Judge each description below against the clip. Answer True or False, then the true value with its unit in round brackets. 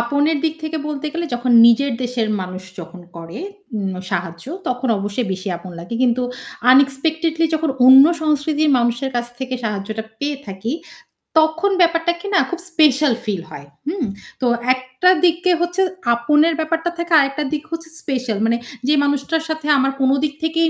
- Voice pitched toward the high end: True (275 Hz)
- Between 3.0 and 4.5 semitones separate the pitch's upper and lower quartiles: False (5.1 semitones)